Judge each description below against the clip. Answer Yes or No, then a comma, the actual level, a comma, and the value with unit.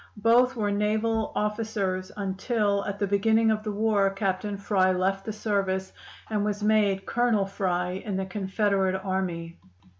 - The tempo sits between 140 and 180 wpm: Yes, average, 150 wpm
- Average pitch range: No, narrow, 2.1 semitones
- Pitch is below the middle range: No, high, 200 Hz